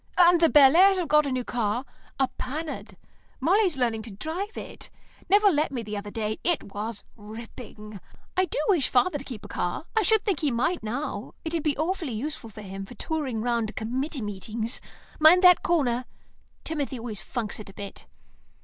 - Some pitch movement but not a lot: No, wide, 6.6 semitones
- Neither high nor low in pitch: No, very high, 260 Hz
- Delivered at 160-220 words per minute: Yes, average, 190 wpm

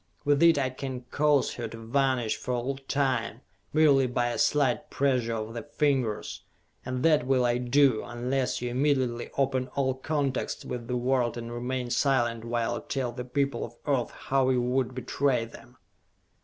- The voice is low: Yes, low, 130 Hz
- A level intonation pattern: Yes, narrow, 2.3 semitones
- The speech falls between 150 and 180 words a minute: Yes, average, 175 wpm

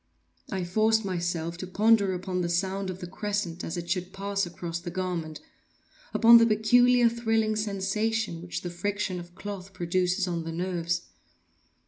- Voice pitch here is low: No, medium, 185 Hz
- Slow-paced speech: No, average, 155 wpm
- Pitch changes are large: No, average, 3.5 semitones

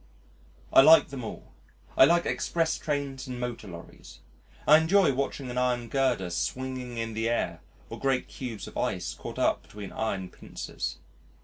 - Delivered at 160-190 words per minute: Yes, average, 165 wpm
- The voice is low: Yes, low, 125 Hz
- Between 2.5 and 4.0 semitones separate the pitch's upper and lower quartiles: Yes, average, 3.5 semitones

